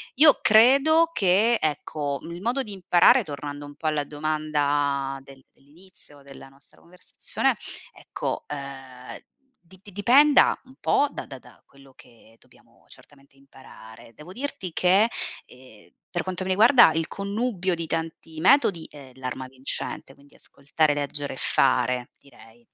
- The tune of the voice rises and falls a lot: Yes, wide, 5.7 semitones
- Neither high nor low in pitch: Yes, medium, 155 Hz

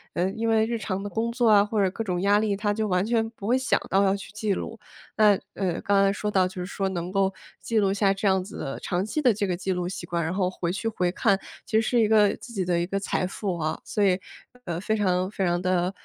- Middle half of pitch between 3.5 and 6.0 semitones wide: No, average, 2.8 semitones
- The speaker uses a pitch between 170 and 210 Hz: Yes, high, 195 Hz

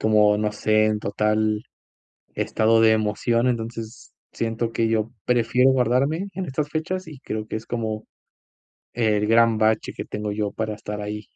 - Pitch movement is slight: Yes, narrow, 2.0 semitones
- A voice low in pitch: Yes, low, 110 Hz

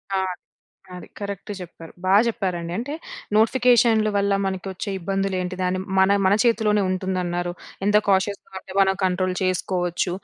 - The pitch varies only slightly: Yes, narrow, 2.1 semitones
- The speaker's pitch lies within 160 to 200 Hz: Yes, high, 190 Hz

